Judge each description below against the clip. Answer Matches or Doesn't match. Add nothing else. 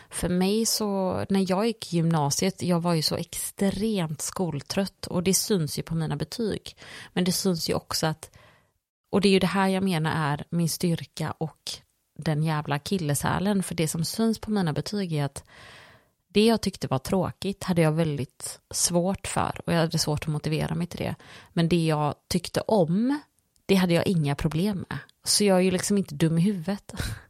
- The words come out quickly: Matches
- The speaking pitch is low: Doesn't match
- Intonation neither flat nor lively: Matches